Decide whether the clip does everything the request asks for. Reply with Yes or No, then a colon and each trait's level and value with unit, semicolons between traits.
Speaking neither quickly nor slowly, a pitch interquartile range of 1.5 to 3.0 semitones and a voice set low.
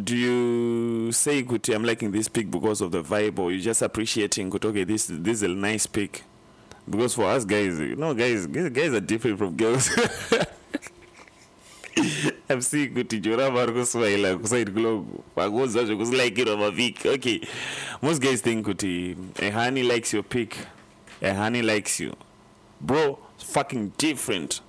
Yes: average, 145 wpm; average, 2.7 semitones; low, 115 Hz